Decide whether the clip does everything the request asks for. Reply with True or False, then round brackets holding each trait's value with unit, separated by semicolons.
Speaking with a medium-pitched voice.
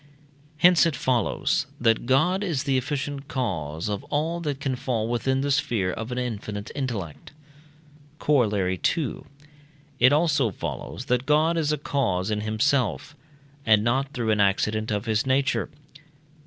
False (125 Hz)